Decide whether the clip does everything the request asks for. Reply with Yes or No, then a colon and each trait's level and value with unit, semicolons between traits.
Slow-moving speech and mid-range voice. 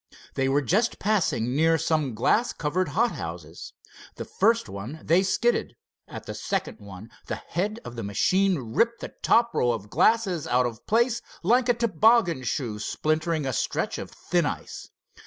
No: average, 165 wpm; medium, 165 Hz